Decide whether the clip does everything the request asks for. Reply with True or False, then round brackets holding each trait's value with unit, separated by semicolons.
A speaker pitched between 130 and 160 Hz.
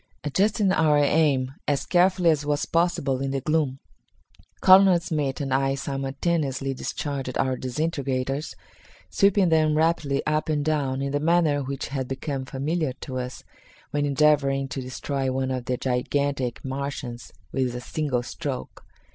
True (140 Hz)